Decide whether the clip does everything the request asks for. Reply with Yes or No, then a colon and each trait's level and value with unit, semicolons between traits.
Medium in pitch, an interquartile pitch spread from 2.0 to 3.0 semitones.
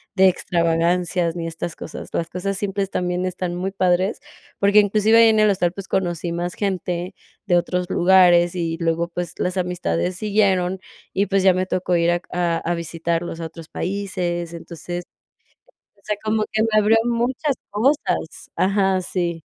Yes: medium, 180 Hz; narrow, 2.5 semitones